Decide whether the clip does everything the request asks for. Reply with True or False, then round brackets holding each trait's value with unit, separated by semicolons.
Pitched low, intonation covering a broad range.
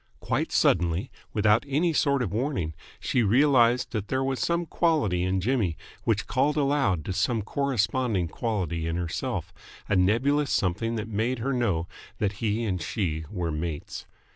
True (110 Hz; 6.3 semitones)